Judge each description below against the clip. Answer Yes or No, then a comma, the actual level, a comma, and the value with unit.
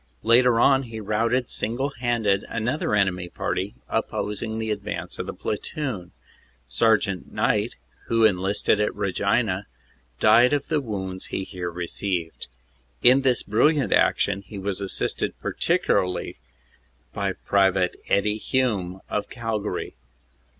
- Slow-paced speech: Yes, slow, 125 wpm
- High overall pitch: No, low, 105 Hz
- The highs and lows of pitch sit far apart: No, average, 3.6 semitones